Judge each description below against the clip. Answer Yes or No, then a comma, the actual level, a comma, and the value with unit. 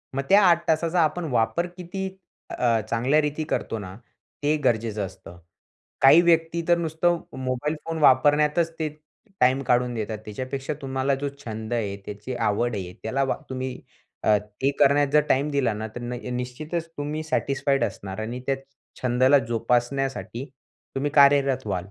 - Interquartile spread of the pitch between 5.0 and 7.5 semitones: No, average, 4.3 semitones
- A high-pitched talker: No, low, 130 Hz